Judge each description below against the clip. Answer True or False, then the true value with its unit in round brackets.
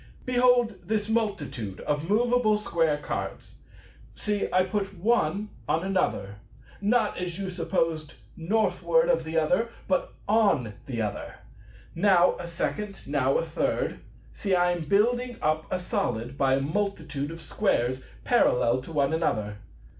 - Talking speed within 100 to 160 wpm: True (140 wpm)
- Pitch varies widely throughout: True (6.0 semitones)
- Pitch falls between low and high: True (180 Hz)